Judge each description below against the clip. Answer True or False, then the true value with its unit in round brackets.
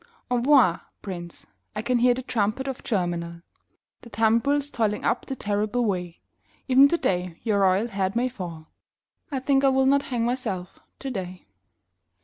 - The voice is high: True (225 Hz)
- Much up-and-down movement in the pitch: True (5.7 semitones)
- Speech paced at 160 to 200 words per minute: False (150 wpm)